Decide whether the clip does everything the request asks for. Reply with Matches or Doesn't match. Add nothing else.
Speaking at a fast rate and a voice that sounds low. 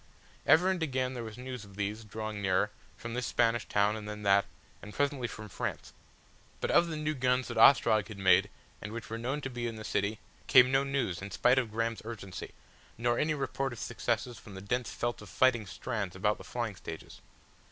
Matches